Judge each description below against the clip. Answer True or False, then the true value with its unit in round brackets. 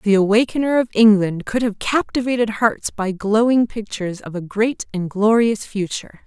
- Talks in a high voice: True (215 Hz)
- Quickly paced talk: False (165 wpm)